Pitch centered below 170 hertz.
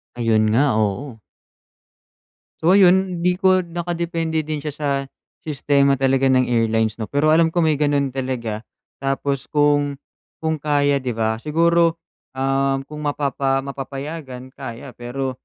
Yes: medium, 140 Hz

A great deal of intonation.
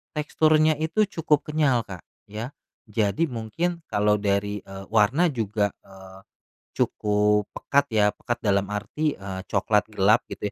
Yes: wide, 6.6 semitones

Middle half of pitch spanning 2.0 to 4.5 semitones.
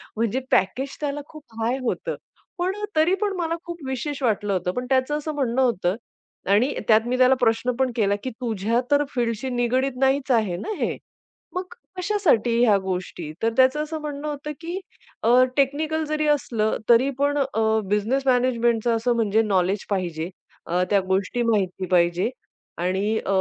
No: wide, 5.4 semitones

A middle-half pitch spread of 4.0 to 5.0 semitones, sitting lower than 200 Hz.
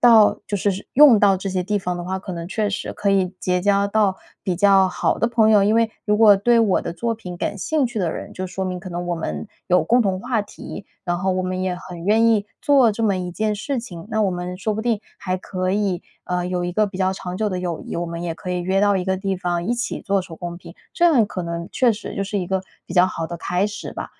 No: average, 2.9 semitones; high, 190 Hz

